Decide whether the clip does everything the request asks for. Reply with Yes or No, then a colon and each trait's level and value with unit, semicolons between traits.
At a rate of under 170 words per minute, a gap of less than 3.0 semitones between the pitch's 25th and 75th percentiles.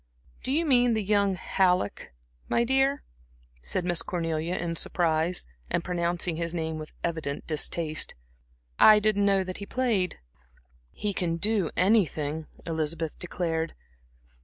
No: slow, 135 wpm; average, 3.9 semitones